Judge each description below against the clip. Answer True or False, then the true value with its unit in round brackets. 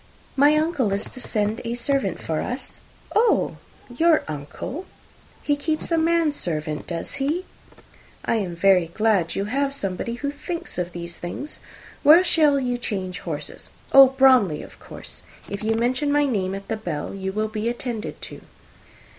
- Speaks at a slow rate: False (165 wpm)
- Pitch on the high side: True (235 Hz)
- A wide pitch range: True (7.0 semitones)